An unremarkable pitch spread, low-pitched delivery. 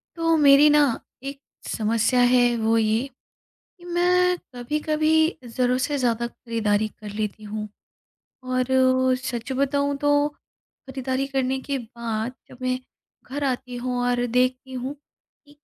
No: average, 3.0 semitones; very high, 255 Hz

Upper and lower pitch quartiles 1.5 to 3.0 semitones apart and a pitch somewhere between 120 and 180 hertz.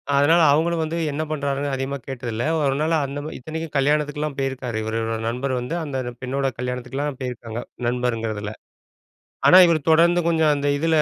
No: average, 3.8 semitones; medium, 140 Hz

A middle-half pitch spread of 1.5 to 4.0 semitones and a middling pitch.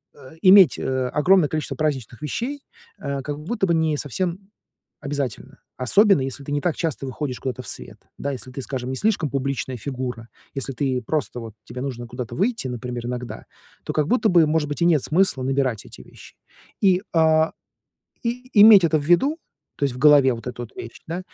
No: average, 4.9 semitones; medium, 145 Hz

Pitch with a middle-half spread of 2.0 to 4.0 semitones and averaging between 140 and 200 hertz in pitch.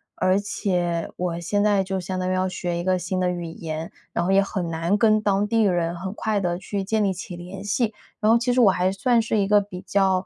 Yes: narrow, 2.5 semitones; high, 190 Hz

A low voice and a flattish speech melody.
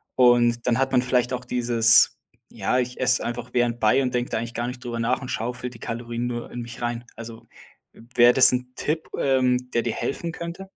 Yes: low, 125 Hz; narrow, 1.2 semitones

